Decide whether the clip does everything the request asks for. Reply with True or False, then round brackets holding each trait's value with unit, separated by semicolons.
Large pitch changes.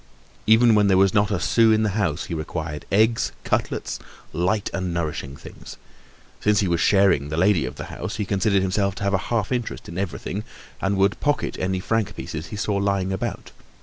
False (3.0 semitones)